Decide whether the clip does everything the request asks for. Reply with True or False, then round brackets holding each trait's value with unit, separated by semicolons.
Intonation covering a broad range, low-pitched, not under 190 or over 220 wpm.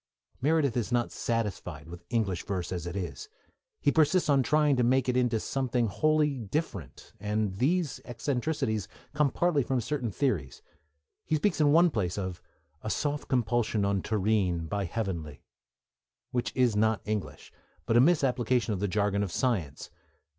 False (5.7 semitones; 115 Hz; 160 wpm)